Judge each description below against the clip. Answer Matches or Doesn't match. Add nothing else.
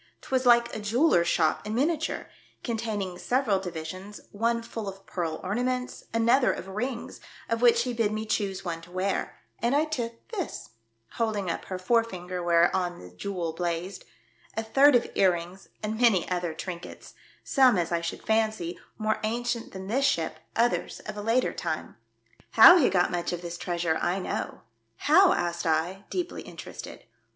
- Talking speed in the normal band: Matches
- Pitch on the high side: Matches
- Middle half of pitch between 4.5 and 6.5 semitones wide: Matches